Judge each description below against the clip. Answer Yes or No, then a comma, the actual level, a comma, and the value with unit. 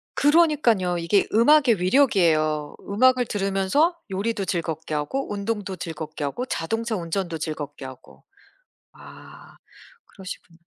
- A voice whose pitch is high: Yes, high, 195 Hz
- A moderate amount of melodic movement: No, wide, 6.0 semitones